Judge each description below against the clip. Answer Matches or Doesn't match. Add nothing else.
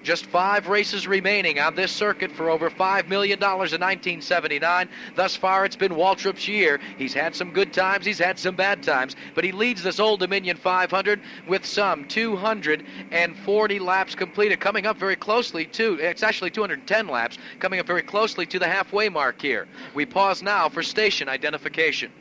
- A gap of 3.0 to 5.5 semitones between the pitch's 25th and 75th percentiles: Doesn't match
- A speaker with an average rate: Matches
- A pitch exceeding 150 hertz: Matches